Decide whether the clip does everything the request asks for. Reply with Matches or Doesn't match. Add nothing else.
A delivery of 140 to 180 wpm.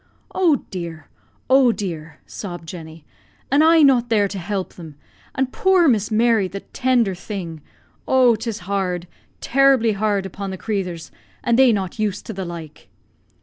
Matches